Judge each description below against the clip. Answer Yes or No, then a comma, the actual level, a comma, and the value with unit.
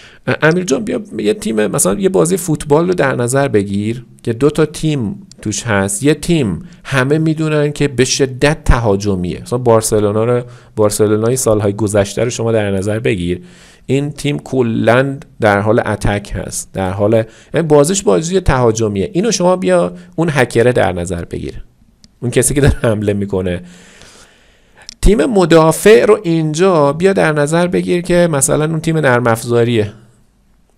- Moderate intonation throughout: No, wide, 6.3 semitones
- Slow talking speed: No, average, 150 wpm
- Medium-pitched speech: No, low, 125 Hz